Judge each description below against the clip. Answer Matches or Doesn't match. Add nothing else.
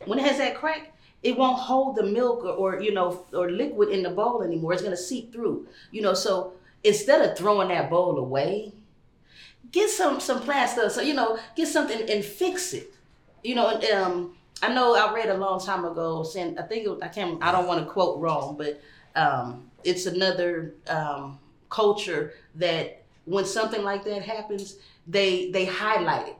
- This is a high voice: Matches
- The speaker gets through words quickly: Doesn't match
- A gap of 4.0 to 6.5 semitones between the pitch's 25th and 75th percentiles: Matches